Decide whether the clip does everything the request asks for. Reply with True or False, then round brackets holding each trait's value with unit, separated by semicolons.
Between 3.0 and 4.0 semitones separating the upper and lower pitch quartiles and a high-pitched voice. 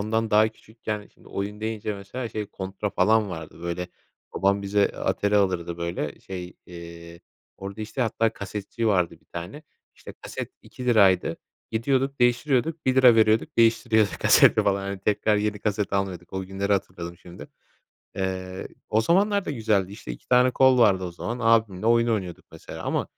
False (3.3 semitones; 105 Hz)